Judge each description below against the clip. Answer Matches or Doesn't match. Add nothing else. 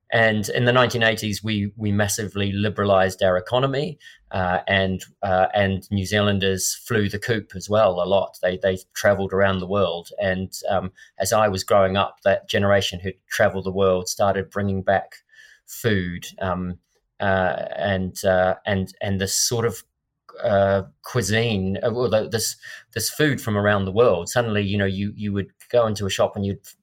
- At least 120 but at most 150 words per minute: Doesn't match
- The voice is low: Matches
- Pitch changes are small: Matches